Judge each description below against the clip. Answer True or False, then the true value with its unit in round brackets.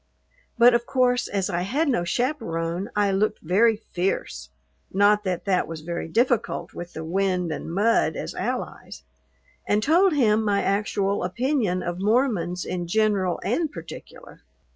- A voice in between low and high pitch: False (200 Hz)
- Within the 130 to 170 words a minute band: True (150 wpm)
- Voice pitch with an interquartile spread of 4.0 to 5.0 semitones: True (4.7 semitones)